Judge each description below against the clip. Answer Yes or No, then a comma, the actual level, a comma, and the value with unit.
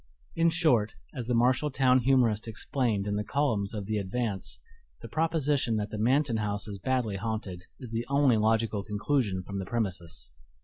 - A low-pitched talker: Yes, low, 115 Hz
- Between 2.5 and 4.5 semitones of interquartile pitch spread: Yes, average, 4.0 semitones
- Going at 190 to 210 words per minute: No, average, 175 wpm